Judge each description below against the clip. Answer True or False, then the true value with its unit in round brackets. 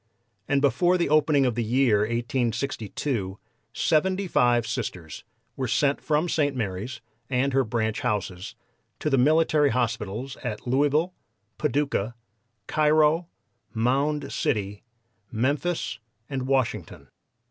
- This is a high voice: False (130 Hz)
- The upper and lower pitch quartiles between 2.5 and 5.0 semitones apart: True (4.5 semitones)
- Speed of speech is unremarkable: False (115 wpm)